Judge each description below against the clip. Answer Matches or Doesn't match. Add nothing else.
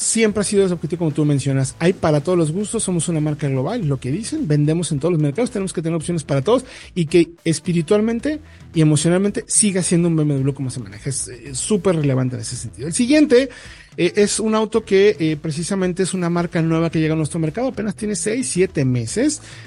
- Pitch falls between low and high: Matches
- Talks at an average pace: Doesn't match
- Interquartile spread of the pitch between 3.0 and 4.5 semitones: Doesn't match